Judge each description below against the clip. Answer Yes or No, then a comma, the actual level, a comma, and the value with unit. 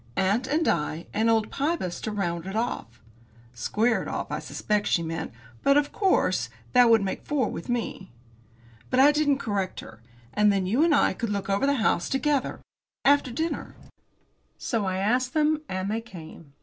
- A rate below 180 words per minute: No, average, 185 wpm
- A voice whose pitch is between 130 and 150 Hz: No, high, 220 Hz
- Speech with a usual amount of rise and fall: No, wide, 6.5 semitones